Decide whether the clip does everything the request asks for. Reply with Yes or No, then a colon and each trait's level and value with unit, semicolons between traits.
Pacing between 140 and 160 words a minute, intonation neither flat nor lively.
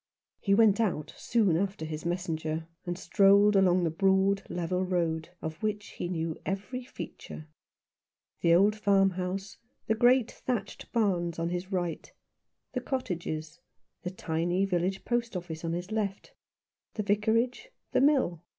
Yes: average, 150 wpm; average, 3.6 semitones